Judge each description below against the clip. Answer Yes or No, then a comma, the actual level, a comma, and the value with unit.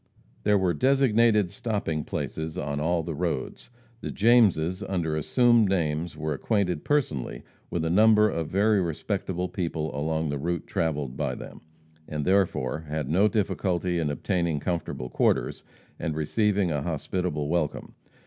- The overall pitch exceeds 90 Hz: No, very low, 85 Hz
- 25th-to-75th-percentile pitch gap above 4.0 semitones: Yes, average, 4.6 semitones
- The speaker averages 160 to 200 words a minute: No, average, 145 wpm